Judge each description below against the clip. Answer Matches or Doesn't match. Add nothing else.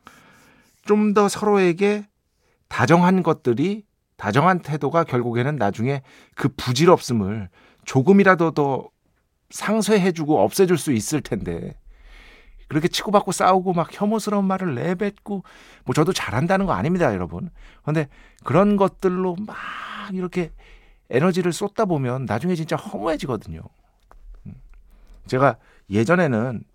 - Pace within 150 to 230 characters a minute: Doesn't match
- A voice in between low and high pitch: Matches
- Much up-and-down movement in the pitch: Matches